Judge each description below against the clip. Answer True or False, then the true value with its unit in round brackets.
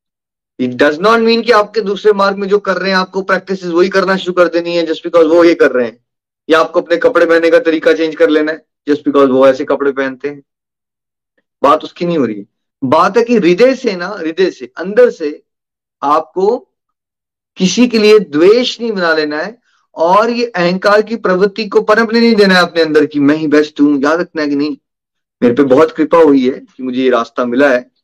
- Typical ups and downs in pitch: False (6.1 semitones)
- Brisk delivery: True (225 wpm)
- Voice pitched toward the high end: False (170 Hz)